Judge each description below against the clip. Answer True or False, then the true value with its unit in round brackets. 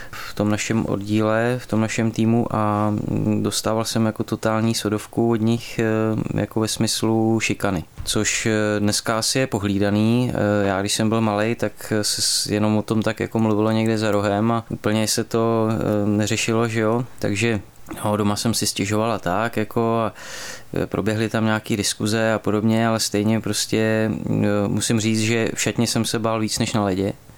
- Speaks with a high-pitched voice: False (110 Hz)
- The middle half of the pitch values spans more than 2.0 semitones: False (1.3 semitones)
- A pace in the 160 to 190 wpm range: True (170 wpm)